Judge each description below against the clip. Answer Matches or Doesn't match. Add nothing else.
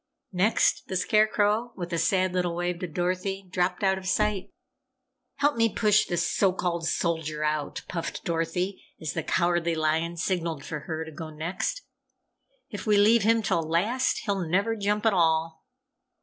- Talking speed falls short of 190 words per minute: Matches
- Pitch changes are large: Doesn't match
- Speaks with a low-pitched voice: Doesn't match